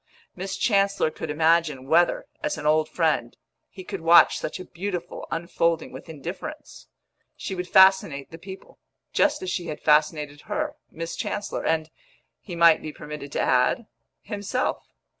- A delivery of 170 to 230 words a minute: No, average, 155 wpm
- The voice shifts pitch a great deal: No, average, 3.5 semitones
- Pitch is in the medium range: Yes, medium, 165 Hz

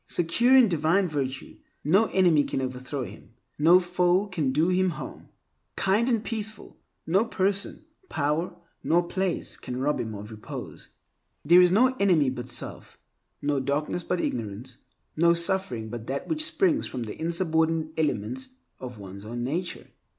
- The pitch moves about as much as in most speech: No, wide, 6.3 semitones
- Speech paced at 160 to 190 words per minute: No, average, 150 wpm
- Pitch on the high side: No, medium, 165 Hz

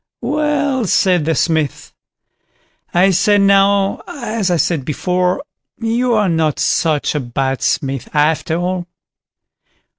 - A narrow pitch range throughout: No, average, 4.7 semitones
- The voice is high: No, medium, 180 Hz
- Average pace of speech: No, slow, 120 wpm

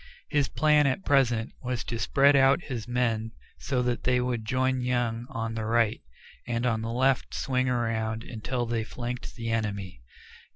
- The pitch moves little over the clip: Yes, narrow, 2.3 semitones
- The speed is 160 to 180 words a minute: Yes, average, 170 wpm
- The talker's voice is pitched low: Yes, low, 120 Hz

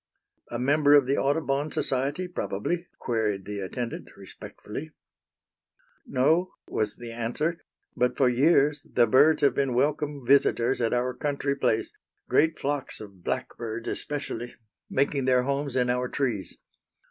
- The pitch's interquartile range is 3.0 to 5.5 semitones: Yes, average, 3.4 semitones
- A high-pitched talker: No, low, 130 Hz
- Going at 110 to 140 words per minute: Yes, slow, 135 wpm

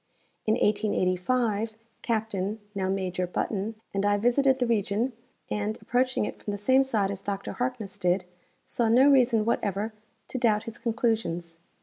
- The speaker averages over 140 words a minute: Yes, average, 150 wpm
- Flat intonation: No, average, 3.2 semitones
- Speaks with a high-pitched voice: Yes, high, 215 Hz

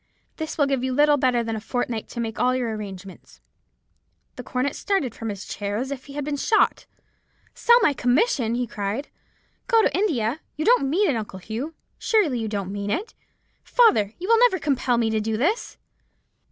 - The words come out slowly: No, average, 200 wpm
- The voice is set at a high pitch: Yes, very high, 255 Hz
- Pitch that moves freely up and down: Yes, wide, 5.9 semitones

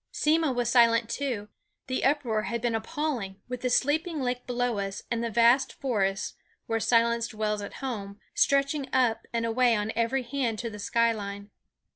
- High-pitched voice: Yes, high, 235 Hz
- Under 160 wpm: No, average, 175 wpm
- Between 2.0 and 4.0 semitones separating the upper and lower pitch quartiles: Yes, average, 2.8 semitones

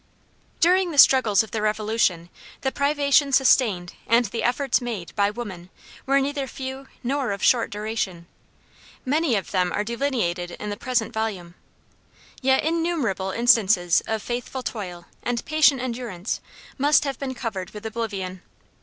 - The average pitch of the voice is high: Yes, high, 230 Hz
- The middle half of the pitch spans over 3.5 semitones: Yes, average, 5.1 semitones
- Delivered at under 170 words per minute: Yes, average, 145 wpm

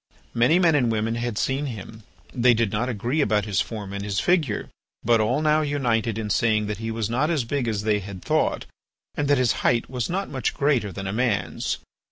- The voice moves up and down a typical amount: Yes, average, 4.2 semitones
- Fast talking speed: Yes, fast, 220 wpm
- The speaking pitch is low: Yes, low, 115 Hz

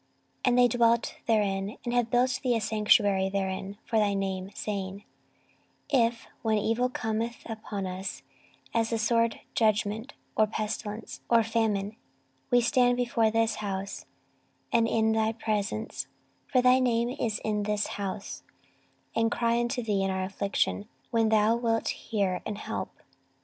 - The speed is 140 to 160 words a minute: Yes, average, 155 wpm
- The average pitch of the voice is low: No, high, 220 Hz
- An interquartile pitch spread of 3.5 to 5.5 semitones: No, narrow, 2.5 semitones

